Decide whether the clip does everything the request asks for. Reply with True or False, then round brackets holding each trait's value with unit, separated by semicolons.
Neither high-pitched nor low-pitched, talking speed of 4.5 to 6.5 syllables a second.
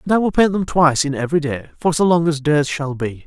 True (155 Hz; 6.3 syllables/s)